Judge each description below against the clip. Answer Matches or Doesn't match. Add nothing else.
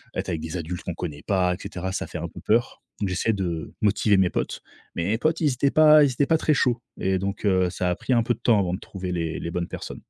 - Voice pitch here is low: Matches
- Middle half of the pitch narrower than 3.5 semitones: Doesn't match